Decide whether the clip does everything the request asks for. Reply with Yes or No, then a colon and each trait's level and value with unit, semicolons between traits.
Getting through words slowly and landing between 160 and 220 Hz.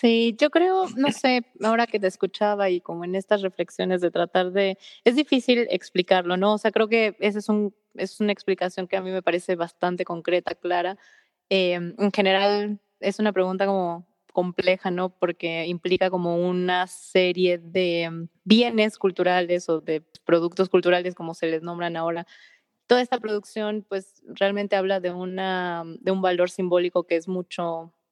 No: average, 170 wpm; medium, 185 Hz